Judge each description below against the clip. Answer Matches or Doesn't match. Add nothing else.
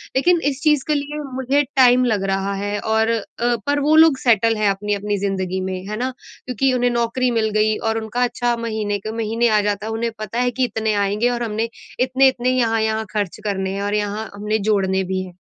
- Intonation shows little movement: Doesn't match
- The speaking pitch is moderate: Doesn't match